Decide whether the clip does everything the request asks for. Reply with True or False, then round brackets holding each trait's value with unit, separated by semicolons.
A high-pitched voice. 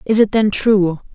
True (205 Hz)